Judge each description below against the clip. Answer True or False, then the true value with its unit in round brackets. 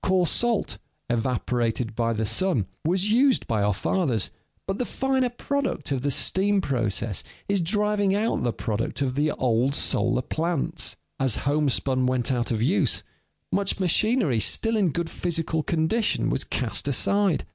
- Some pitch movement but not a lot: False (8.6 semitones)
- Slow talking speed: False (155 wpm)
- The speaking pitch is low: False (150 Hz)